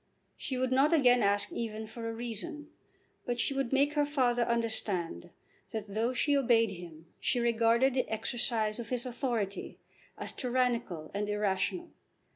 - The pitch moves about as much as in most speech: Yes, average, 3.2 semitones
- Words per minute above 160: No, average, 155 wpm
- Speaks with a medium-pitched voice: No, high, 235 Hz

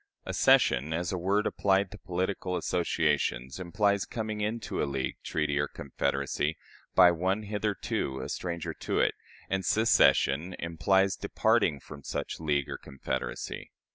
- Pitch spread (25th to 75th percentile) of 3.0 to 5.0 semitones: No, wide, 5.5 semitones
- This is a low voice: Yes, very low, 90 Hz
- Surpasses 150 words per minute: No, average, 140 wpm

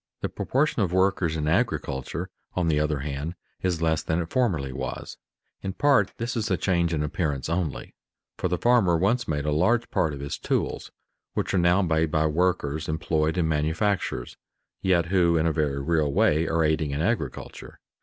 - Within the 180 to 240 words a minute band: Yes, average, 185 wpm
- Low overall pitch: Yes, very low, 80 Hz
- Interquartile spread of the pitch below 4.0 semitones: Yes, average, 3.4 semitones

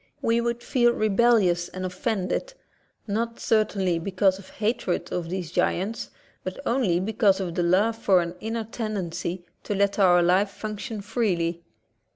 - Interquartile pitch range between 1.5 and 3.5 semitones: No, average, 3.9 semitones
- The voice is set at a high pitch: Yes, high, 200 Hz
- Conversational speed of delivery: Yes, average, 150 wpm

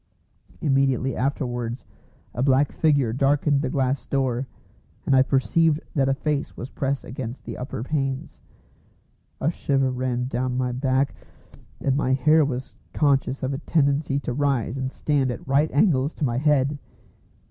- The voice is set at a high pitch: No, low, 135 Hz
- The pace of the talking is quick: No, average, 155 wpm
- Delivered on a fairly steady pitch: Yes, narrow, 1.8 semitones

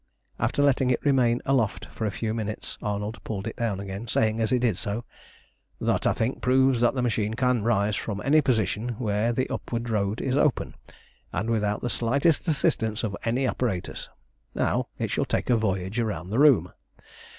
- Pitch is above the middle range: No, low, 115 Hz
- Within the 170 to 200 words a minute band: Yes, average, 185 wpm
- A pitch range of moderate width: Yes, average, 3.2 semitones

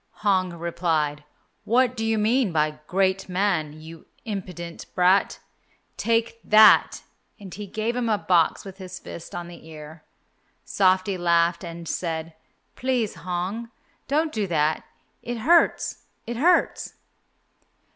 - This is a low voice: No, medium, 185 Hz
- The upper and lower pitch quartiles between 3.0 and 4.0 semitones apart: No, average, 4.8 semitones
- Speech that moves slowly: Yes, slow, 130 wpm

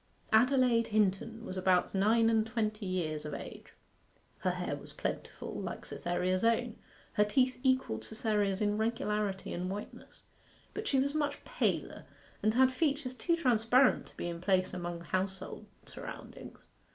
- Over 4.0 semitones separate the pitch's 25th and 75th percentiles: Yes, average, 5.0 semitones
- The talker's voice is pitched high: Yes, high, 215 Hz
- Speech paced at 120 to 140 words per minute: No, average, 150 wpm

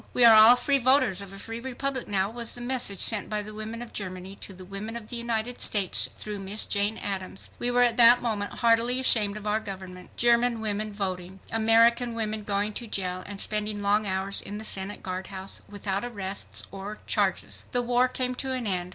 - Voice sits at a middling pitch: No, high, 215 Hz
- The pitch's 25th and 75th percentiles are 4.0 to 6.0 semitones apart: No, average, 3.2 semitones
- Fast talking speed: Yes, fast, 210 wpm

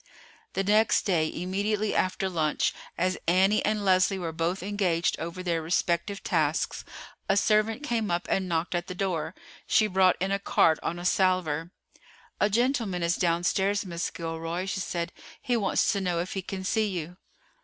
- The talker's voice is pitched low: No, medium, 185 Hz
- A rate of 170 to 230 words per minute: Yes, average, 175 wpm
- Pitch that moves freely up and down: No, average, 2.8 semitones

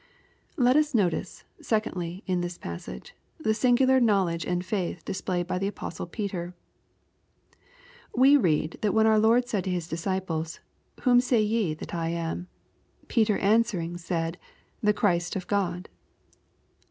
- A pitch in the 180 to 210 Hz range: Yes, high, 190 Hz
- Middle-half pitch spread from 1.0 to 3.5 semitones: No, average, 4.2 semitones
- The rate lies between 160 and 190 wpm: No, average, 145 wpm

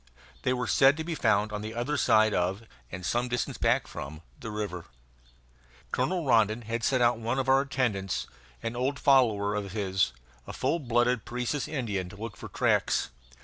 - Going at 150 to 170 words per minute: No, average, 185 wpm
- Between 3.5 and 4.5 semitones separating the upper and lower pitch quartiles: Yes, average, 3.8 semitones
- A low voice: Yes, low, 115 Hz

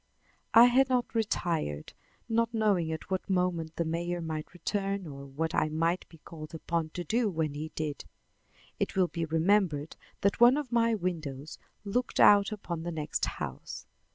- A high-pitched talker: No, medium, 175 Hz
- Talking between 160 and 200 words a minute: Yes, average, 170 wpm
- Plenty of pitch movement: No, average, 4.6 semitones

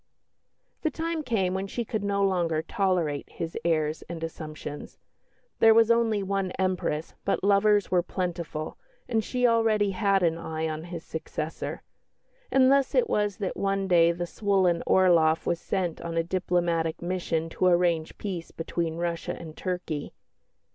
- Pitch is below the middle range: No, medium, 180 Hz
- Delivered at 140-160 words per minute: Yes, average, 155 wpm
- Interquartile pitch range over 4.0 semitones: No, average, 3.5 semitones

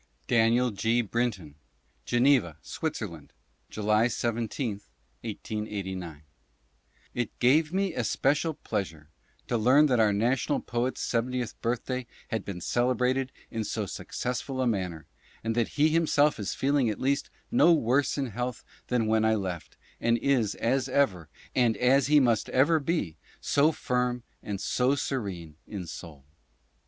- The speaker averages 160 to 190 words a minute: No, average, 140 wpm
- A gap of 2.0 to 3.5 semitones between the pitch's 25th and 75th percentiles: No, average, 4.2 semitones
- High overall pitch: No, low, 120 Hz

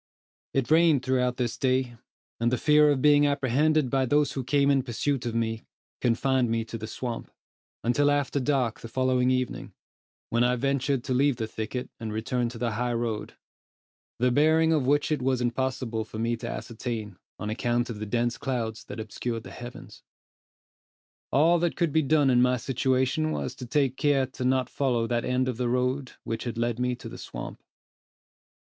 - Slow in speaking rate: No, average, 190 wpm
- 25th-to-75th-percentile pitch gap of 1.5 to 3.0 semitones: Yes, average, 2.7 semitones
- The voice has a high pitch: No, low, 125 Hz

